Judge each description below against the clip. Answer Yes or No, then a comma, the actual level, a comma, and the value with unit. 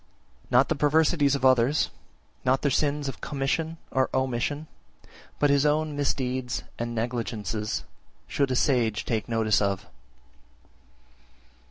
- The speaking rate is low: Yes, slow, 130 wpm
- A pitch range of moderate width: Yes, average, 3.5 semitones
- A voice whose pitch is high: No, low, 130 Hz